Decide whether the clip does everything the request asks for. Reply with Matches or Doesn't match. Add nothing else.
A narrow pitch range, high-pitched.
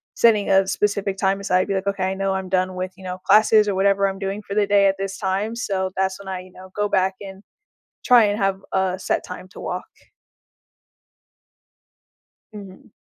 Matches